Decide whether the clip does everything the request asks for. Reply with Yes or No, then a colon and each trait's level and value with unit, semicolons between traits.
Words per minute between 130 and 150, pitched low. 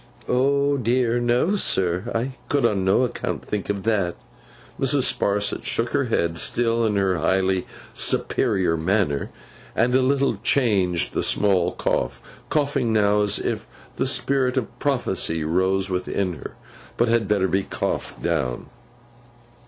Yes: average, 140 wpm; low, 105 Hz